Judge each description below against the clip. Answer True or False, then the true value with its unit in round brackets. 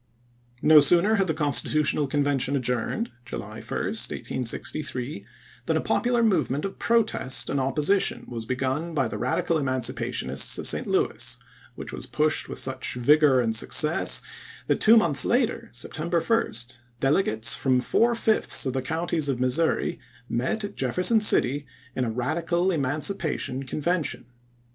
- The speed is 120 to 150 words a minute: True (145 wpm)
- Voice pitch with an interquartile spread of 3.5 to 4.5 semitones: False (5.1 semitones)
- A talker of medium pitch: True (145 Hz)